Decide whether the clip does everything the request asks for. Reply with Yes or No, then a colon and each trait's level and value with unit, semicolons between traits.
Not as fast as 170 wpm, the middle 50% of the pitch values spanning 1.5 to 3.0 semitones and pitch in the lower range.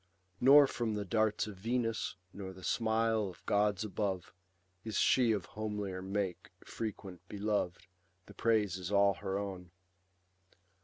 Yes: average, 140 wpm; narrow, 2.6 semitones; low, 105 Hz